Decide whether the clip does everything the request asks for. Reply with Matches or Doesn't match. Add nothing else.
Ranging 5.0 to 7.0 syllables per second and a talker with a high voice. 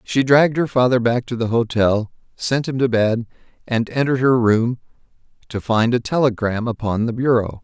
Doesn't match